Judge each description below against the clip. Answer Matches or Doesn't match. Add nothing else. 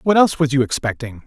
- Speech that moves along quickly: Matches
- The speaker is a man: Matches